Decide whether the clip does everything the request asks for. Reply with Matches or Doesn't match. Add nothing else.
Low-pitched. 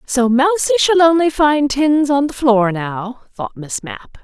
Doesn't match